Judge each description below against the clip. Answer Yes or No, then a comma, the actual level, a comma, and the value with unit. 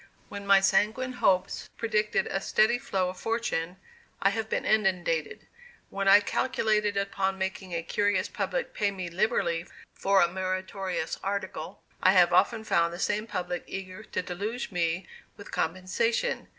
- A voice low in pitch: No, high, 195 Hz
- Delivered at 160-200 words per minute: No, average, 150 wpm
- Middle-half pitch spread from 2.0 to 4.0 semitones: Yes, narrow, 2.6 semitones